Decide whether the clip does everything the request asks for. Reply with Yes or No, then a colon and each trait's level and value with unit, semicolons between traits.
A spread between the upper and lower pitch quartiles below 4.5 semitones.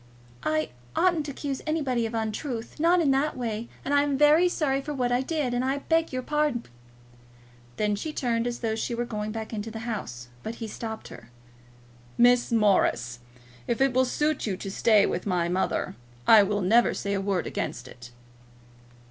No: average, 4.8 semitones